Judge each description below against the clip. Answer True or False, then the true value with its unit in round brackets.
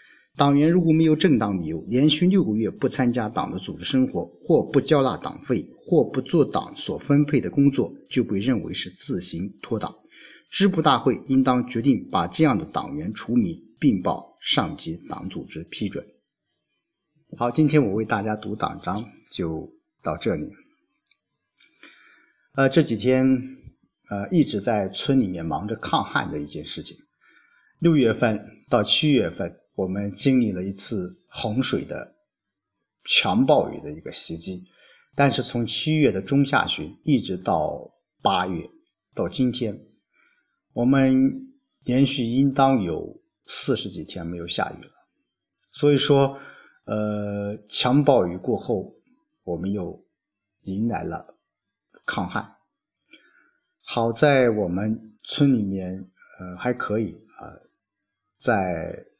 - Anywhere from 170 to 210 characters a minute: True (200 characters per minute)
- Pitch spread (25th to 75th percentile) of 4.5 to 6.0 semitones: True (5.7 semitones)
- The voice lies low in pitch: True (130 Hz)